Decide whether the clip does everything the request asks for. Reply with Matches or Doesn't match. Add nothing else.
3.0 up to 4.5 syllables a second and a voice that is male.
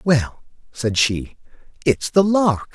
Matches